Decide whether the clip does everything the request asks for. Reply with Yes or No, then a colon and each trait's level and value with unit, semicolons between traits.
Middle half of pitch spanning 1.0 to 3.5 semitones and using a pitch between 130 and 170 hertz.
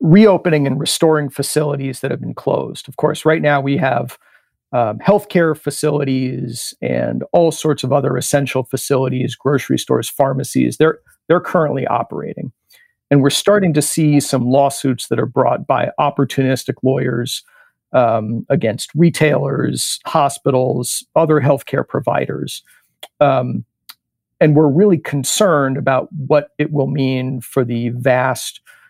Yes: average, 2.8 semitones; medium, 140 Hz